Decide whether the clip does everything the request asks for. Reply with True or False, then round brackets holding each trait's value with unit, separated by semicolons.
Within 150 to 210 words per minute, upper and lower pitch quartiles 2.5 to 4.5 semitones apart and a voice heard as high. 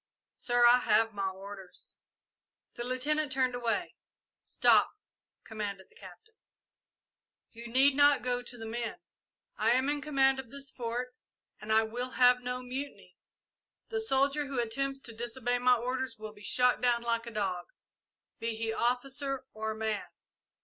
True (155 wpm; 2.9 semitones; 245 Hz)